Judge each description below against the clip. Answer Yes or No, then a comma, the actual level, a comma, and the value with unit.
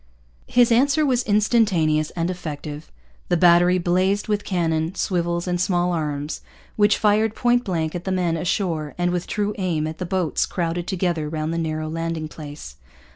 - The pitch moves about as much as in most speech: Yes, average, 3.6 semitones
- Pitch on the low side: No, medium, 175 Hz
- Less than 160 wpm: No, average, 170 wpm